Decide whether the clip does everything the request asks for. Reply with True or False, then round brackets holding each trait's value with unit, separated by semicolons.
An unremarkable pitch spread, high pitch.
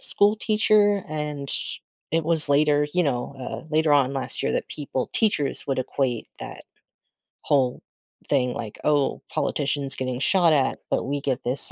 False (3.0 semitones; 145 Hz)